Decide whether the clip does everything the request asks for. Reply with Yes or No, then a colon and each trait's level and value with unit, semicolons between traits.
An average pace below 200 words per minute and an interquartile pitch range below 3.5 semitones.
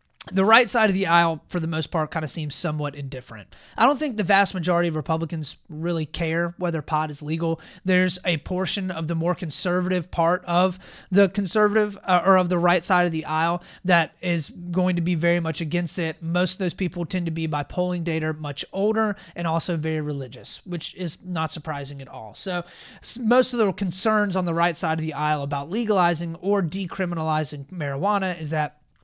No: fast, 205 wpm; narrow, 2.6 semitones